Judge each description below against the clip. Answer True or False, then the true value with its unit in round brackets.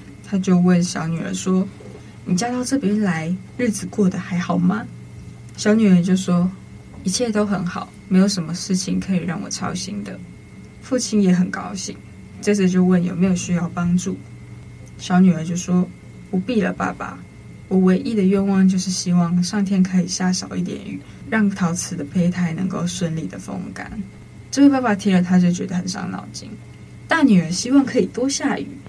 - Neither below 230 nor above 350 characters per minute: True (260 characters per minute)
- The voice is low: False (185 Hz)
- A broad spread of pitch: False (2.0 semitones)